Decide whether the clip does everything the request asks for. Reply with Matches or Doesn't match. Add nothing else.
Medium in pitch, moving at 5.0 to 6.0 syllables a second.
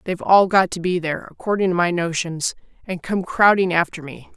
Matches